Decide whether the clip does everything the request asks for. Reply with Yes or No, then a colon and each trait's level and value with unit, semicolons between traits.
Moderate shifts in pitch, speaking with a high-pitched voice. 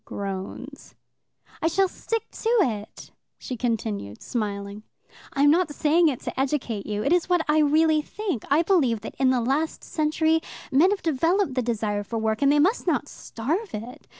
No: wide, 6.3 semitones; very high, 280 Hz